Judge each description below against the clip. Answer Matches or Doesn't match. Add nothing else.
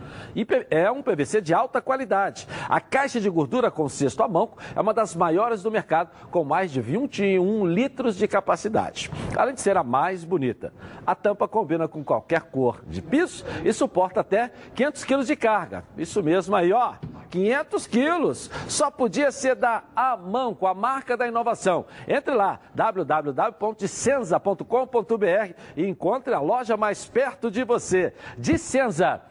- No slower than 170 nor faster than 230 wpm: Doesn't match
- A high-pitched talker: Matches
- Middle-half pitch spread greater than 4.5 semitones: Matches